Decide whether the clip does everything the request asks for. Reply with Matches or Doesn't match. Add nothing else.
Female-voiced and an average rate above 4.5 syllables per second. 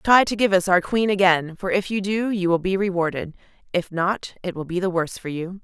Matches